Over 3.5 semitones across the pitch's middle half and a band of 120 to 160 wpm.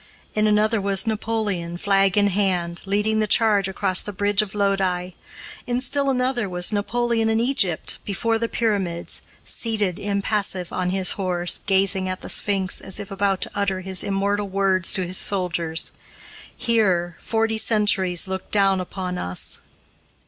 No: narrow, 2.5 semitones; average, 155 wpm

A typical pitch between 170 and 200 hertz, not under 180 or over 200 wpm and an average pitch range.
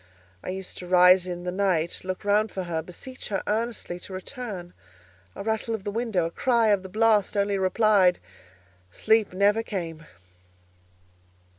No: high, 190 Hz; average, 155 wpm; average, 3.4 semitones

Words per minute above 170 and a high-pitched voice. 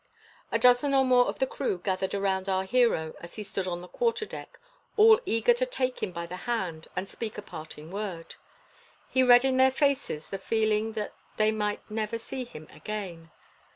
Yes: average, 190 wpm; high, 215 Hz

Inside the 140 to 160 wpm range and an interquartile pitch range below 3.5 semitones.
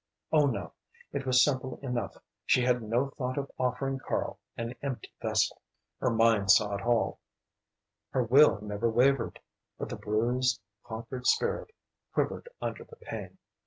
Yes: average, 150 wpm; average, 2.8 semitones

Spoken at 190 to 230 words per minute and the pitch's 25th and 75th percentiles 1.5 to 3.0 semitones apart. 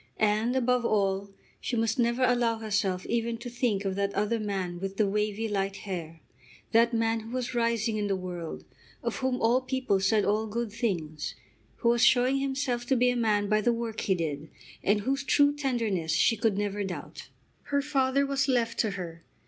No: average, 195 wpm; average, 3.6 semitones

